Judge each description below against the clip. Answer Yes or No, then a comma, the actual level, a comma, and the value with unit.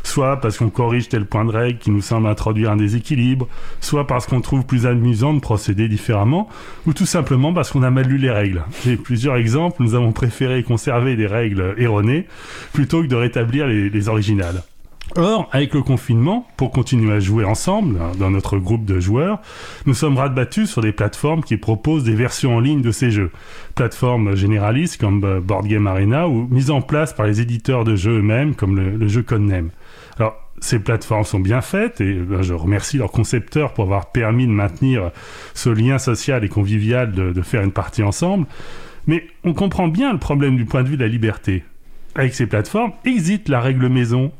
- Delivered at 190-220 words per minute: Yes, average, 200 wpm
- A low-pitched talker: Yes, low, 120 Hz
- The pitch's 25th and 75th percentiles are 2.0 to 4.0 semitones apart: No, average, 4.5 semitones